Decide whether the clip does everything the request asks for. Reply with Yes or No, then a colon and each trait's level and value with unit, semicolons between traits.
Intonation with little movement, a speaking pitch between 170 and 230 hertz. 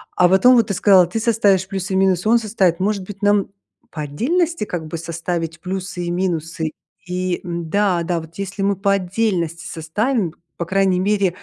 No: average, 3.0 semitones; medium, 185 Hz